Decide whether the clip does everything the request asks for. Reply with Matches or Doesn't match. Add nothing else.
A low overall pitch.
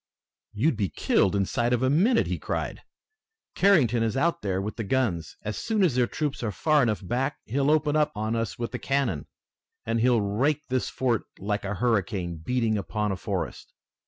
Matches